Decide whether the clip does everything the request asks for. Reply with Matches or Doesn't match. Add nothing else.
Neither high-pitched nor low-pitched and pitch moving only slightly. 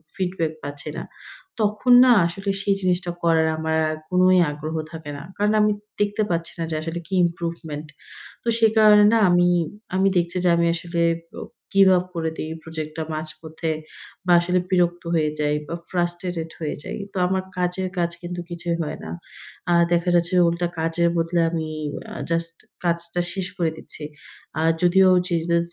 Matches